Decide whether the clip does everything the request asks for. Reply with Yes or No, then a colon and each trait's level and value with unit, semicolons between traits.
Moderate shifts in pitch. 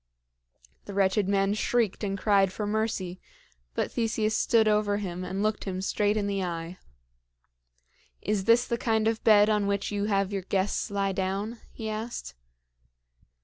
No: narrow, 1.9 semitones